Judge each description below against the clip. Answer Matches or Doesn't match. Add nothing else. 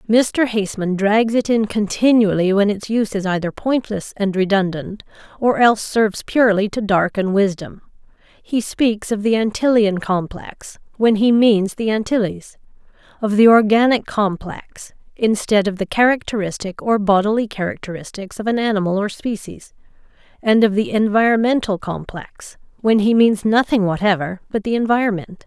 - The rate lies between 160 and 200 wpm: Doesn't match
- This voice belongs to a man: Doesn't match